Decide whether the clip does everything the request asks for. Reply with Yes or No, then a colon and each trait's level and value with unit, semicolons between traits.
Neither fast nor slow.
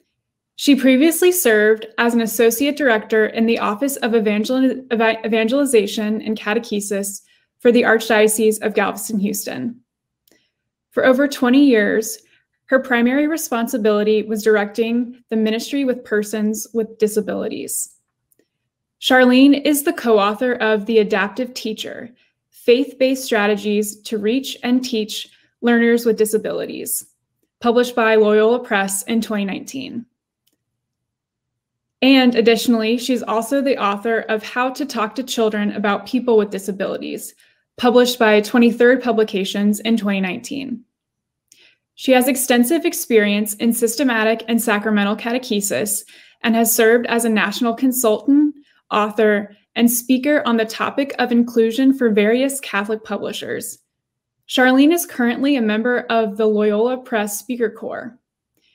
No: slow, 125 wpm